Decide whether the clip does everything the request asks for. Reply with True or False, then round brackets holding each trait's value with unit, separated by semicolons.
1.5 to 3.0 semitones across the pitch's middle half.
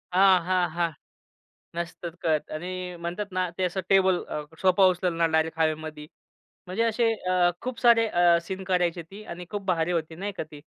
True (2.4 semitones)